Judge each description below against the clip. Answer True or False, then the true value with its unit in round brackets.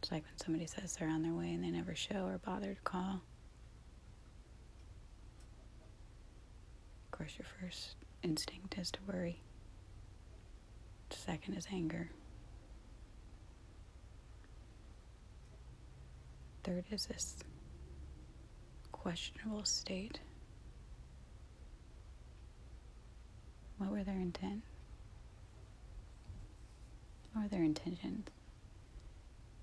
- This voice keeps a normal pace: False (85 wpm)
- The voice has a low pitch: True (105 Hz)